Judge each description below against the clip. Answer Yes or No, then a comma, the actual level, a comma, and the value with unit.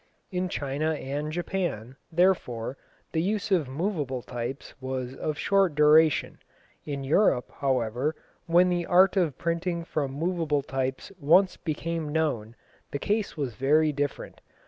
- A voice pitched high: No, medium, 155 Hz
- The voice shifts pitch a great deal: No, average, 4.6 semitones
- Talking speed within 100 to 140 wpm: Yes, slow, 135 wpm